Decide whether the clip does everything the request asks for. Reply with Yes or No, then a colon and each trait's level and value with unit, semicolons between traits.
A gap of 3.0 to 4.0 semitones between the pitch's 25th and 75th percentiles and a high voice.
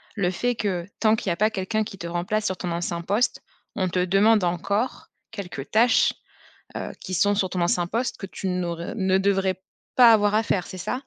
Yes: average, 3.3 semitones; high, 195 Hz